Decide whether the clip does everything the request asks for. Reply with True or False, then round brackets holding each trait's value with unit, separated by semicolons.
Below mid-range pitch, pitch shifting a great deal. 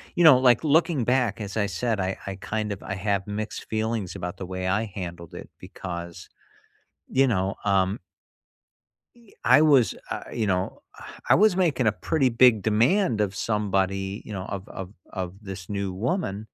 False (105 Hz; 4.5 semitones)